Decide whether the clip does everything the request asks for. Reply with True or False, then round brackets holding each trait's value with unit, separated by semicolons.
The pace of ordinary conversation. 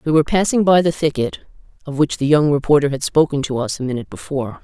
False (235 wpm)